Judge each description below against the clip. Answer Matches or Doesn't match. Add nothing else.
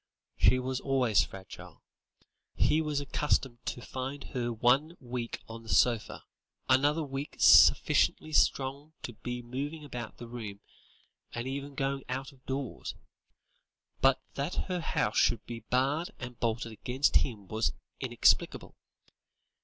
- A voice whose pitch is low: Matches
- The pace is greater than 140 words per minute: Doesn't match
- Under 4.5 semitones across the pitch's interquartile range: Matches